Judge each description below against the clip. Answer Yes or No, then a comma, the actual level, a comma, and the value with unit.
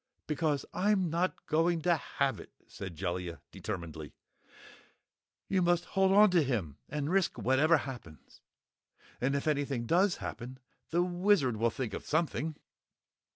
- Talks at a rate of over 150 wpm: No, average, 140 wpm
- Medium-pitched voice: Yes, medium, 150 Hz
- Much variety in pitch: Yes, wide, 6.8 semitones